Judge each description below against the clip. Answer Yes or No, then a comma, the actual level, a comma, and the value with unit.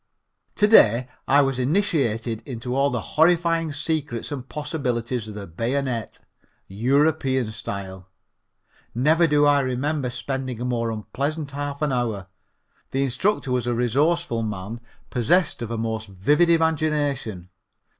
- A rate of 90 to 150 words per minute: Yes, slow, 135 wpm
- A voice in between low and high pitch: No, low, 130 Hz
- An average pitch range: Yes, average, 4.4 semitones